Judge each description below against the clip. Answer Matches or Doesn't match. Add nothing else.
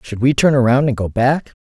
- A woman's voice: Doesn't match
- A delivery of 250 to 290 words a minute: Matches